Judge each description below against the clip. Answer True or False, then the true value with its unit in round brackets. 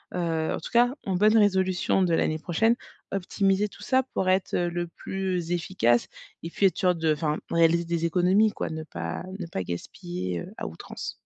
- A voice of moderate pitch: True (175 Hz)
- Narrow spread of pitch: False (3.1 semitones)